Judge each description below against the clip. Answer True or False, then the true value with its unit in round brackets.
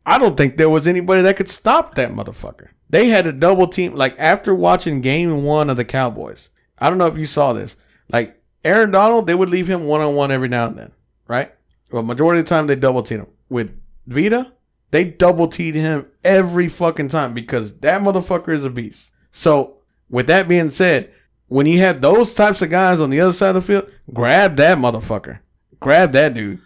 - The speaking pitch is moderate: True (160 Hz)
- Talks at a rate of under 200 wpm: False (205 wpm)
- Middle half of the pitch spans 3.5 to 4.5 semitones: False (5.5 semitones)